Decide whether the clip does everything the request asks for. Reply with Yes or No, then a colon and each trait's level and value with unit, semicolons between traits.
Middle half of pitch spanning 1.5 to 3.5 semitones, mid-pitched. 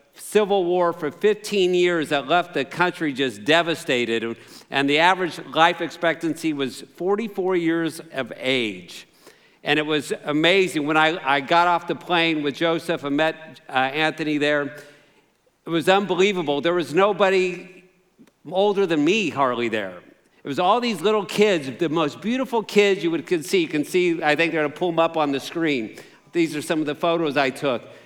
No: average, 4.0 semitones; medium, 165 Hz